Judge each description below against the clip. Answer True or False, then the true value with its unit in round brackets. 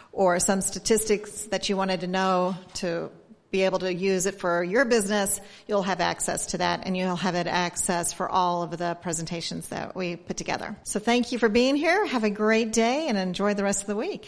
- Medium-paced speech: False (225 wpm)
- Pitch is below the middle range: False (190 Hz)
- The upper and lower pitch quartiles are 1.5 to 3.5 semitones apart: True (2.8 semitones)